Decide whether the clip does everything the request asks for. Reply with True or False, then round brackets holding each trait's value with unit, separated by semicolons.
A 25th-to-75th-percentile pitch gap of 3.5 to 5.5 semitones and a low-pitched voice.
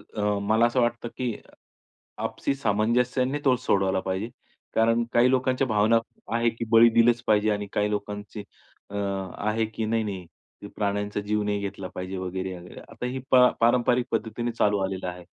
False (2.6 semitones; 110 Hz)